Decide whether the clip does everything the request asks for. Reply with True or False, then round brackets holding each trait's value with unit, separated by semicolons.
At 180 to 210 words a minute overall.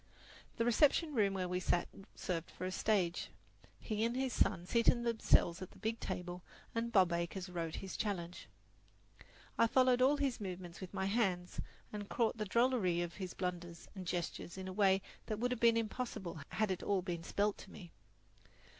True (185 wpm)